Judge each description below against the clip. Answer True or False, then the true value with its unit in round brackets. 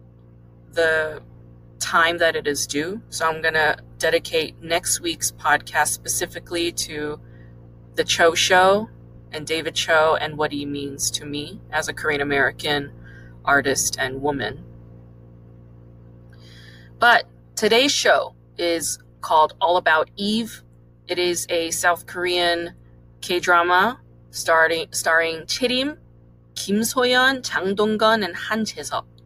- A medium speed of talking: False (120 wpm)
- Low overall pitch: False (150 Hz)